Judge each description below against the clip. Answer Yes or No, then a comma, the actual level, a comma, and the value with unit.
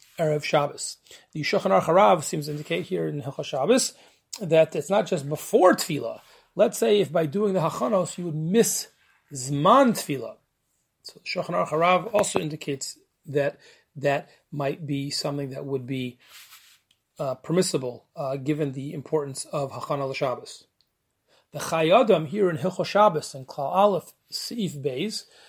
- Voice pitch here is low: No, medium, 155 Hz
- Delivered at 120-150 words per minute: Yes, average, 145 wpm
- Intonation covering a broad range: No, average, 4.8 semitones